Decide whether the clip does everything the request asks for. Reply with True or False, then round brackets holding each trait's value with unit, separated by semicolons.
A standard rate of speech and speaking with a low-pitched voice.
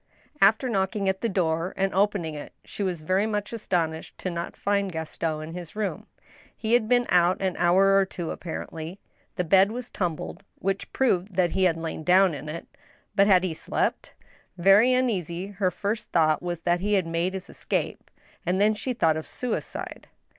False (190 wpm; 185 Hz)